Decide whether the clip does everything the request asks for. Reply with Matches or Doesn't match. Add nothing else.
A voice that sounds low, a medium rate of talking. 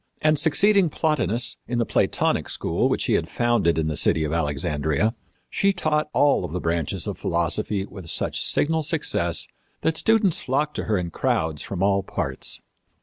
Matches